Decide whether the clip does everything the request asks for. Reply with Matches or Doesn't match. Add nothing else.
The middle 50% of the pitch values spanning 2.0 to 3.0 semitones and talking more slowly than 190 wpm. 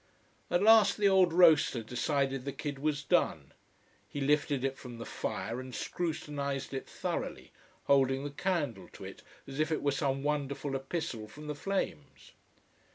Matches